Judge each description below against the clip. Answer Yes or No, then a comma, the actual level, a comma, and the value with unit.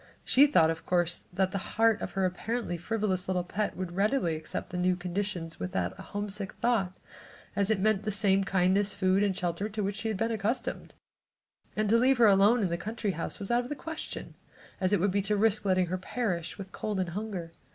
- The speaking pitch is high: Yes, high, 195 Hz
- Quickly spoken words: Yes, fast, 220 wpm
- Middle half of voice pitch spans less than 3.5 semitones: Yes, average, 2.9 semitones